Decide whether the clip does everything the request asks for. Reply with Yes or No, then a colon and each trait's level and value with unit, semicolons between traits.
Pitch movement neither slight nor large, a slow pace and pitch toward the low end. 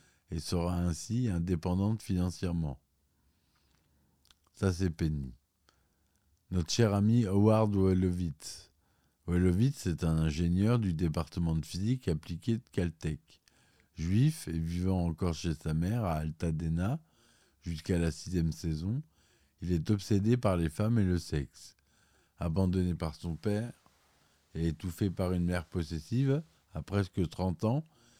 Yes: average, 3.6 semitones; slow, 130 wpm; very low, 90 Hz